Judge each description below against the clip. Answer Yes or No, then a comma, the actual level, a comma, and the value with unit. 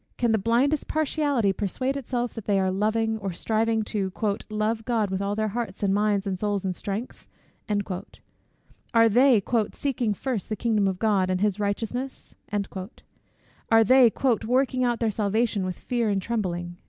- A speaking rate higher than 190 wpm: No, average, 165 wpm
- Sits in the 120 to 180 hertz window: No, high, 215 Hz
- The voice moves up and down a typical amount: Yes, average, 3.2 semitones